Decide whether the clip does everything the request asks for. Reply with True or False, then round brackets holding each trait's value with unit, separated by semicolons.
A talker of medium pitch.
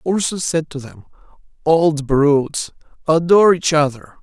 True (155 Hz)